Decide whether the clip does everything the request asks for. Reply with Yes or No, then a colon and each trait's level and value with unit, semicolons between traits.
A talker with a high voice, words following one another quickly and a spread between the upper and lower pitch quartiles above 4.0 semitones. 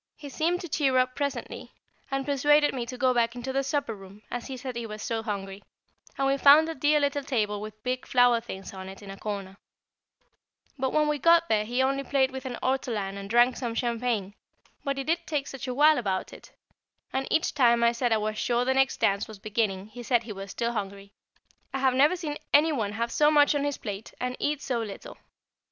Yes: very high, 250 Hz; fast, 230 wpm; average, 4.4 semitones